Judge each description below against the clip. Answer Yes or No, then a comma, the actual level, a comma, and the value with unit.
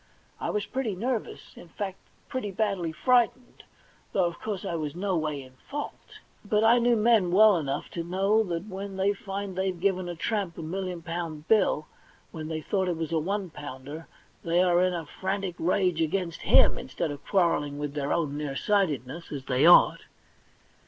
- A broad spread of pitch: No, average, 4.0 semitones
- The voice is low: No, medium, 180 Hz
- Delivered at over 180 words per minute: Yes, average, 190 wpm